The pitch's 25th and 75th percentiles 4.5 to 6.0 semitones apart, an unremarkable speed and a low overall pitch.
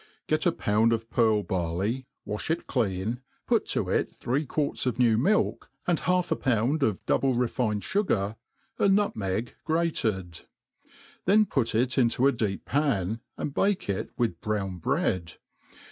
Yes: wide, 5.4 semitones; average, 160 wpm; low, 115 Hz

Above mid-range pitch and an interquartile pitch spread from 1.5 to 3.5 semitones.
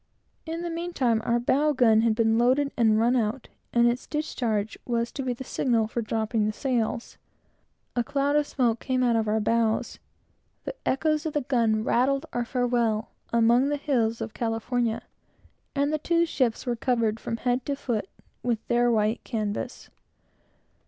Yes: high, 240 Hz; average, 3.1 semitones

